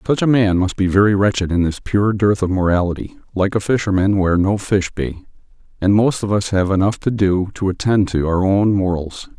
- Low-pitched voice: Yes, low, 100 Hz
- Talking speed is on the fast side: Yes, fast, 215 wpm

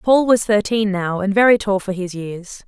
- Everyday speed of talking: No, fast, 225 wpm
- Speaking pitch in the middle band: No, high, 205 Hz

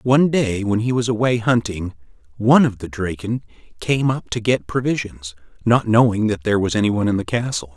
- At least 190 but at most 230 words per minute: Yes, average, 195 wpm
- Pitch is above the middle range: No, low, 110 Hz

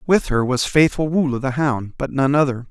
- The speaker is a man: Yes, male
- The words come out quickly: Yes, fast, 220 wpm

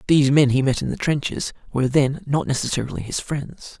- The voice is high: No, medium, 140 Hz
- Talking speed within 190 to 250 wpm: Yes, fast, 205 wpm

